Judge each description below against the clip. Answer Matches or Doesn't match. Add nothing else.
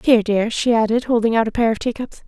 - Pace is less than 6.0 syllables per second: Doesn't match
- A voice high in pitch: Matches